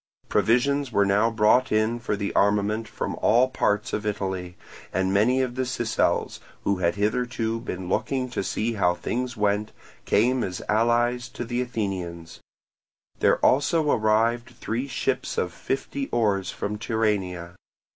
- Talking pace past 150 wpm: No, average, 145 wpm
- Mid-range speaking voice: No, low, 110 Hz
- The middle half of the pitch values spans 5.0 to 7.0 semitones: No, average, 3.3 semitones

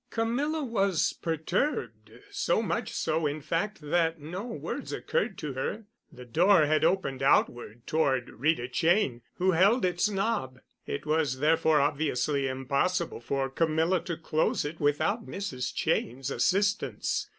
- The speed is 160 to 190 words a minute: No, slow, 135 wpm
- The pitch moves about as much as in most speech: No, wide, 5.7 semitones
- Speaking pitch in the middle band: Yes, medium, 160 Hz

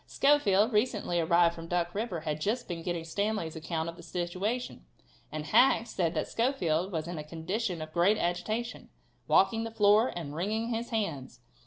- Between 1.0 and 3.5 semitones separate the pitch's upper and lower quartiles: No, average, 4.9 semitones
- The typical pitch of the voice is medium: Yes, medium, 180 Hz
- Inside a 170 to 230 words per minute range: Yes, average, 175 wpm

